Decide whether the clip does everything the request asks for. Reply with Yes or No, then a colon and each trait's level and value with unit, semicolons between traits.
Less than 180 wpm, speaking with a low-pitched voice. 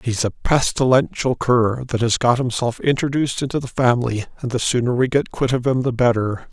No: average, 200 wpm; low, 125 Hz